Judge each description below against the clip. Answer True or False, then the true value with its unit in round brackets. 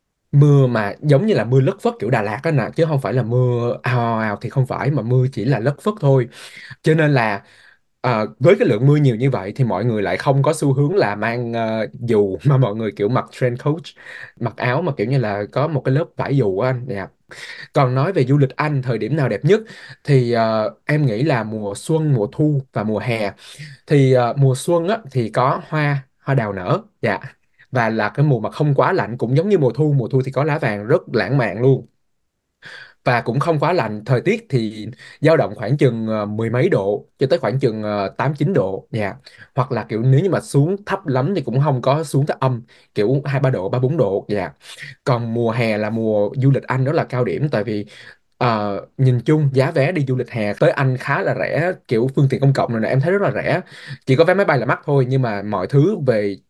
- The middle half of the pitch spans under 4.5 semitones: True (3.9 semitones)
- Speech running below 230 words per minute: False (250 wpm)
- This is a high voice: False (130 Hz)